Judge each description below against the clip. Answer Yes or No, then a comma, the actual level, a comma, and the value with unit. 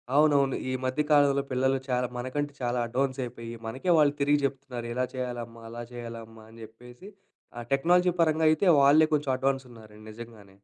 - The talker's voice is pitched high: No, low, 130 Hz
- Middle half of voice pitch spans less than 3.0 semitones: No, average, 3.3 semitones